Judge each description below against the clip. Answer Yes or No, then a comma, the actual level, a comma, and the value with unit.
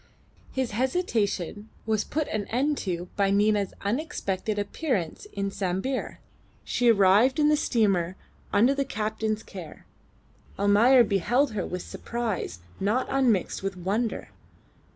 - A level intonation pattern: No, average, 4.2 semitones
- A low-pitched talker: No, high, 215 Hz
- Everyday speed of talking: No, slow, 125 wpm